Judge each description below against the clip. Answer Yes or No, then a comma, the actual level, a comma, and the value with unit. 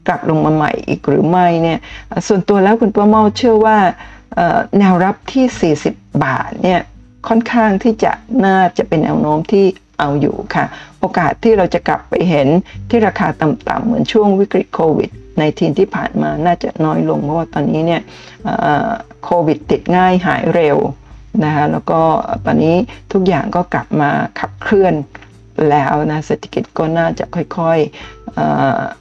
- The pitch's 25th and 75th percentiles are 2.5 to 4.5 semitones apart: No, average, 5.2 semitones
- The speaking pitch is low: No, medium, 175 Hz